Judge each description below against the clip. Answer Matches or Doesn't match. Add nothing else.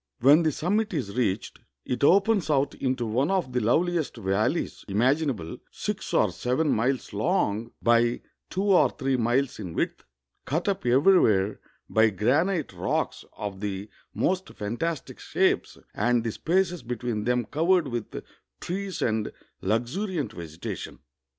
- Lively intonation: Matches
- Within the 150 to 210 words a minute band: Doesn't match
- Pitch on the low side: Matches